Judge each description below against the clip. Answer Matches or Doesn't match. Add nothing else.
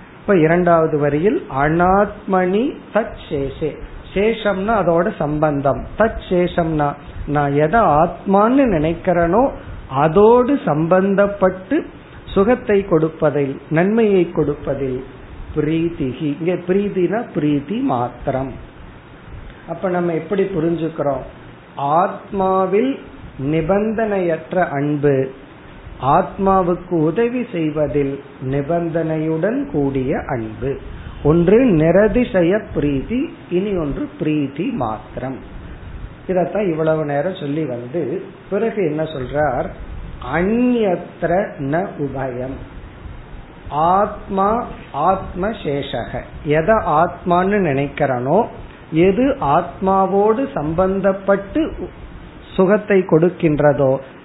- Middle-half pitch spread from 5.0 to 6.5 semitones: Matches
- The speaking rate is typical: Doesn't match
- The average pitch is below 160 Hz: Doesn't match